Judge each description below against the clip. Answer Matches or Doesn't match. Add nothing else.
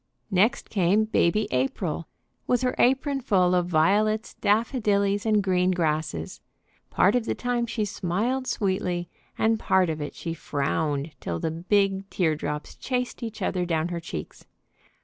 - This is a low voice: Doesn't match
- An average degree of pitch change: Matches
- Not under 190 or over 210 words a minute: Doesn't match